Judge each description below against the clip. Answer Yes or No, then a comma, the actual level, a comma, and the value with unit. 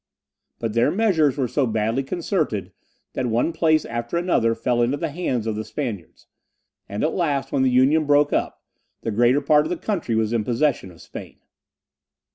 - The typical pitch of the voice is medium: No, low, 130 Hz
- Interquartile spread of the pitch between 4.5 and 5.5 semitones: Yes, average, 5.1 semitones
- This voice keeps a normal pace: Yes, average, 190 wpm